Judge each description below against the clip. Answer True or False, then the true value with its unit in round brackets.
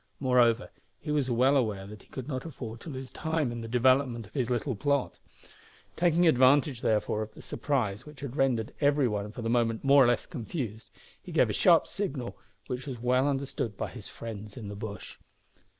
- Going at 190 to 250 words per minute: True (200 wpm)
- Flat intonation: False (3.7 semitones)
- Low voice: True (125 Hz)